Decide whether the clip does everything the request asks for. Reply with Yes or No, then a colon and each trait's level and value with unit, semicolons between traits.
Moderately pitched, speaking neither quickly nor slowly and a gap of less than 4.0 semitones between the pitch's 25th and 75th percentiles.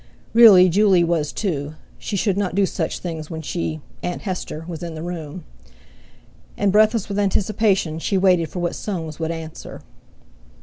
Yes: medium, 175 Hz; average, 150 wpm; average, 3.6 semitones